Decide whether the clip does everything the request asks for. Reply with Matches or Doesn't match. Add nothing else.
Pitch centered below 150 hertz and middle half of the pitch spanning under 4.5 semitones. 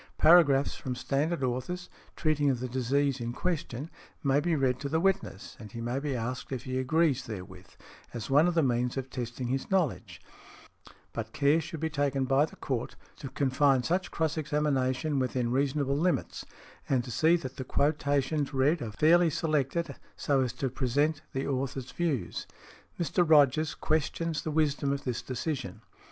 Matches